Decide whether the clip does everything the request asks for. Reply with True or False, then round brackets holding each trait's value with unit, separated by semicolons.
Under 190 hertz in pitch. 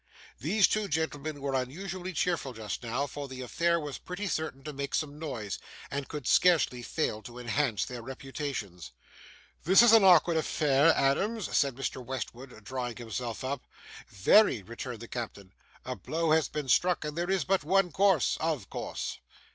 True (140 Hz)